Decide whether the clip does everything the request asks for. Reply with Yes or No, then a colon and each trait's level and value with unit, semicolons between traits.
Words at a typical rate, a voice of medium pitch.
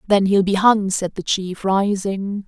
No: average, 195 wpm; high, 195 Hz